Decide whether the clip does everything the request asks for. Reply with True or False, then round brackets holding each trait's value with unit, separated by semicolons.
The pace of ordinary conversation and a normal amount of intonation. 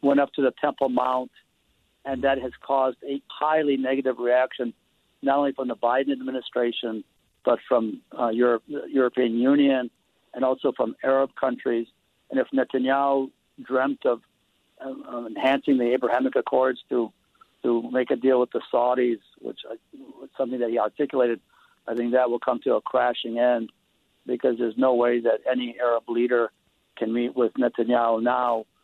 False (165 wpm; 1.9 semitones)